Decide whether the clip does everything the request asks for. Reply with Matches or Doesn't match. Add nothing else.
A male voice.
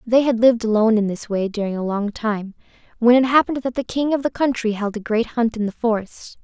Doesn't match